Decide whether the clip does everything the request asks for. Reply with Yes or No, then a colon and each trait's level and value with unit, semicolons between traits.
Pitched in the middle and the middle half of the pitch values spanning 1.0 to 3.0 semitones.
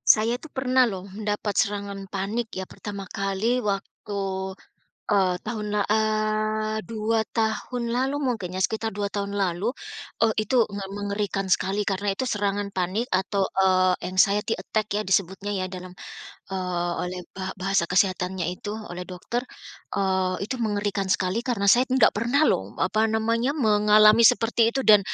No: high, 205 Hz; narrow, 2.4 semitones